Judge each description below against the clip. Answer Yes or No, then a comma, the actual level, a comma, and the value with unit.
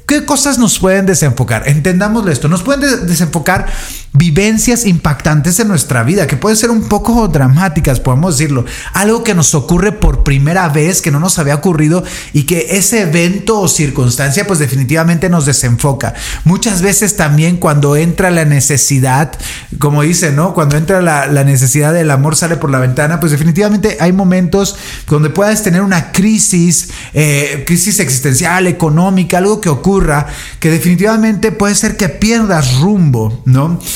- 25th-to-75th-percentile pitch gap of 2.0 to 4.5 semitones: No, average, 4.9 semitones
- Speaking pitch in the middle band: Yes, medium, 170 Hz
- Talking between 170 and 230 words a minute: No, average, 160 wpm